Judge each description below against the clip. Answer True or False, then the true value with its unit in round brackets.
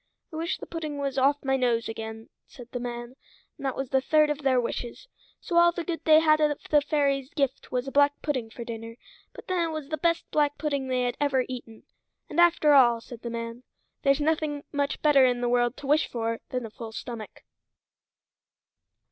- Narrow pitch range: False (3.8 semitones)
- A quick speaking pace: True (215 wpm)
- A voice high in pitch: True (275 Hz)